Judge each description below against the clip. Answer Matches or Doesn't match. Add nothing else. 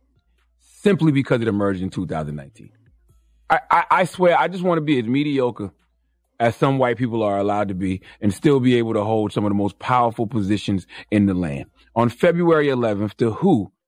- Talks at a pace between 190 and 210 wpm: Matches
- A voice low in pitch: Matches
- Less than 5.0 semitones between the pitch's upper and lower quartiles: Doesn't match